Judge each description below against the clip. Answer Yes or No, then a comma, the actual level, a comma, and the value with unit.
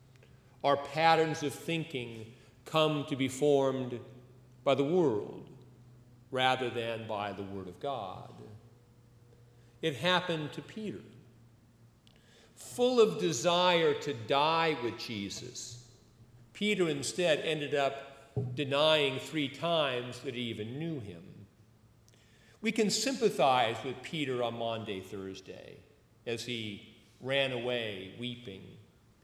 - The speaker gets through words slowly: Yes, slow, 110 wpm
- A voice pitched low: Yes, low, 125 Hz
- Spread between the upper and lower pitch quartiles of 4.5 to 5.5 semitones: No, average, 4.1 semitones